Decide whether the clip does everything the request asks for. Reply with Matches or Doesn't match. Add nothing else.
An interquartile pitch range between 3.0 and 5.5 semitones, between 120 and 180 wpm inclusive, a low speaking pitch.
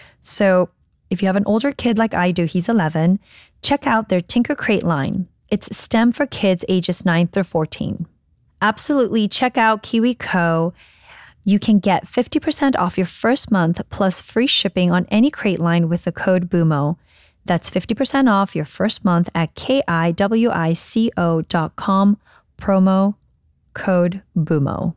Doesn't match